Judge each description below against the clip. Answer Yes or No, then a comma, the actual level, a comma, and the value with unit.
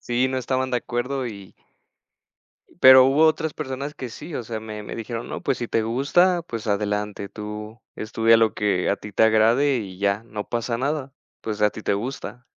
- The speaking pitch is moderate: No, low, 115 Hz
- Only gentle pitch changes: No, average, 3.6 semitones